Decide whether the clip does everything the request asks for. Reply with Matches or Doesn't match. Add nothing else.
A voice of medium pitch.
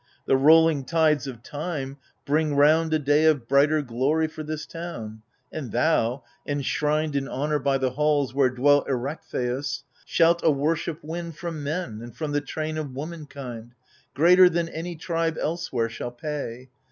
Matches